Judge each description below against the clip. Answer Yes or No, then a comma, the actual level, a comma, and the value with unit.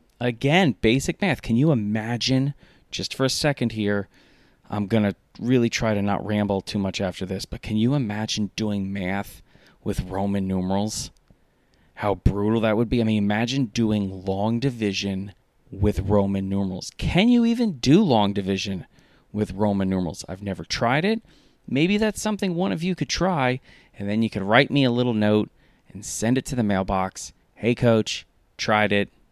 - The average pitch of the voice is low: Yes, low, 110 Hz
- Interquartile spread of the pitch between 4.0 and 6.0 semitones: Yes, average, 4.6 semitones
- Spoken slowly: No, average, 175 wpm